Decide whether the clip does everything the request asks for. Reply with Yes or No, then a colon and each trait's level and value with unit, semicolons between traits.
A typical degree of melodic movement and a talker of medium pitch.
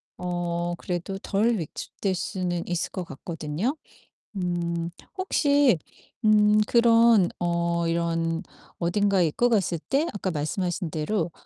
Yes: average, 3.7 semitones; medium, 180 Hz